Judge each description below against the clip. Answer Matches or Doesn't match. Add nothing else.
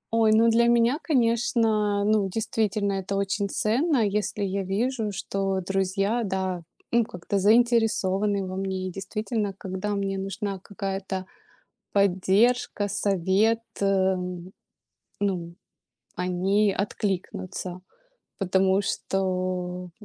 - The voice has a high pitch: Matches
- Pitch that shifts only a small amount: Matches